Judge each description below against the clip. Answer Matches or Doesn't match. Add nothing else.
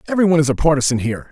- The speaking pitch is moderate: Matches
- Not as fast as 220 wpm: Doesn't match